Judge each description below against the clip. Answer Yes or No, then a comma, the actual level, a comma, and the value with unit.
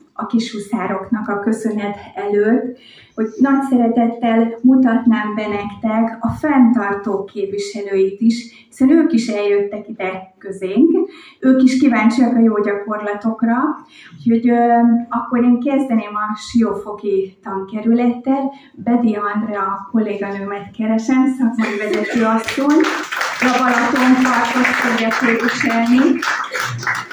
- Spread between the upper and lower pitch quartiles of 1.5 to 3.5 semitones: Yes, average, 3.1 semitones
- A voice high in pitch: Yes, high, 230 Hz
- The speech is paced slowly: Yes, slow, 100 wpm